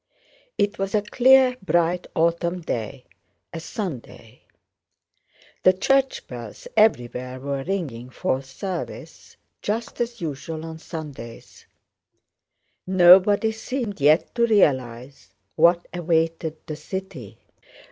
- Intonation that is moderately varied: No, wide, 6.5 semitones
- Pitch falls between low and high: Yes, medium, 170 Hz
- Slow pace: Yes, slow, 105 wpm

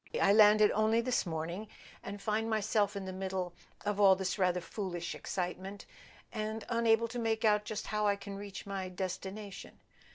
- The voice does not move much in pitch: Yes, narrow, 2.3 semitones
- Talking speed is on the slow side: No, average, 170 wpm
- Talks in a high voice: Yes, high, 205 Hz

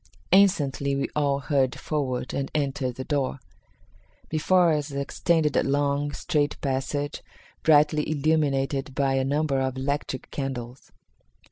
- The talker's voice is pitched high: No, medium, 140 Hz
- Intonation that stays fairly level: Yes, narrow, 1.9 semitones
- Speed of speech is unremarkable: No, slow, 125 wpm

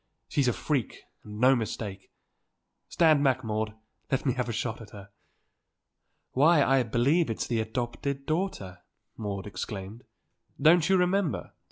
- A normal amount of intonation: Yes, average, 5.0 semitones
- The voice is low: Yes, low, 125 Hz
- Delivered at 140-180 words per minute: Yes, average, 150 wpm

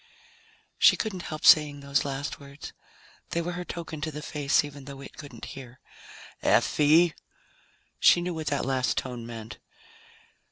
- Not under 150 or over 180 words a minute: Yes, average, 155 wpm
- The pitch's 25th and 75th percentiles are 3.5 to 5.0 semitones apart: No, average, 2.7 semitones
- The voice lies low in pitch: No, medium, 145 Hz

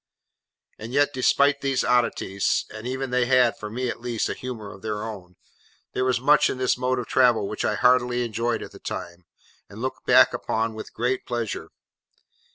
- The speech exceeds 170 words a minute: Yes, average, 180 wpm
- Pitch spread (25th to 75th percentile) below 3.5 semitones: Yes, average, 2.7 semitones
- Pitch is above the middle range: No, low, 120 Hz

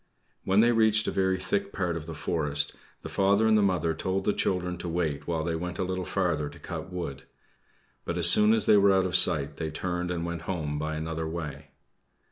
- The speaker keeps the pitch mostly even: No, average, 3.1 semitones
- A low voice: Yes, very low, 90 Hz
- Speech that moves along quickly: Yes, fast, 220 wpm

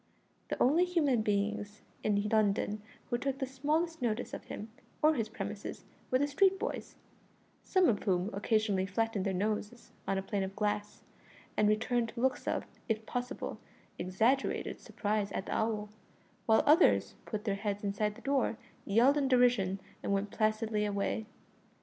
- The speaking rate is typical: Yes, average, 160 wpm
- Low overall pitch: No, high, 215 Hz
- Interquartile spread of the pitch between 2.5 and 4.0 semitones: Yes, average, 3.7 semitones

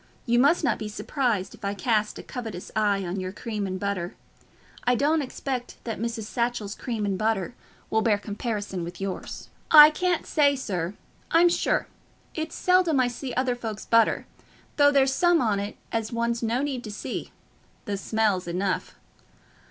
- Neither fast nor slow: Yes, average, 170 wpm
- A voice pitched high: Yes, high, 225 Hz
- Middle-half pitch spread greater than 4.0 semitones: Yes, average, 4.6 semitones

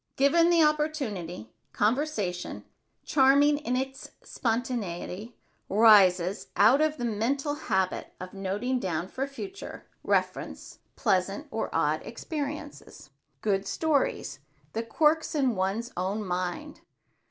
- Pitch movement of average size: No, wide, 7.0 semitones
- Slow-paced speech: Yes, slow, 115 wpm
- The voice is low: No, high, 240 Hz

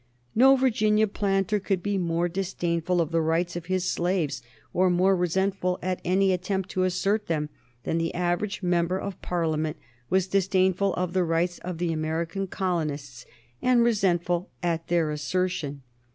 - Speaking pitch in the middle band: Yes, medium, 180 Hz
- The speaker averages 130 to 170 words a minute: Yes, average, 155 wpm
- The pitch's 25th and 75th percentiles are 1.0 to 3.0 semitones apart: Yes, narrow, 2.5 semitones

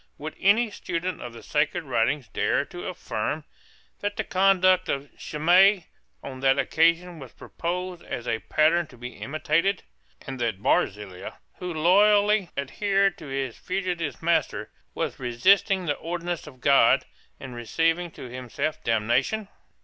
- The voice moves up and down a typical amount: No, wide, 5.7 semitones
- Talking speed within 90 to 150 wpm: Yes, average, 140 wpm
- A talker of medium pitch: Yes, medium, 165 Hz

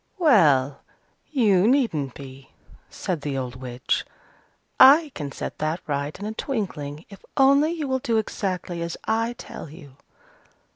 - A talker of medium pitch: Yes, medium, 180 Hz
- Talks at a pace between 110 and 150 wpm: Yes, average, 145 wpm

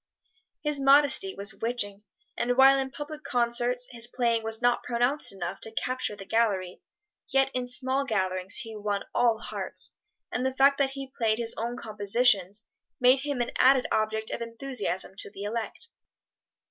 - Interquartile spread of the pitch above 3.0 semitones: Yes, average, 3.4 semitones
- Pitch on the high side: Yes, high, 240 Hz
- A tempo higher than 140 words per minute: Yes, average, 165 wpm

